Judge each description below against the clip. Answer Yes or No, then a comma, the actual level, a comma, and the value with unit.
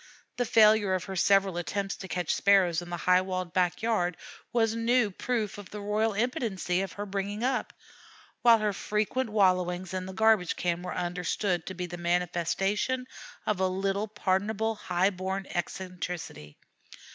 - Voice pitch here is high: Yes, high, 195 Hz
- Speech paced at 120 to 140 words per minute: No, average, 165 wpm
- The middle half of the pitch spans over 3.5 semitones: No, average, 3.0 semitones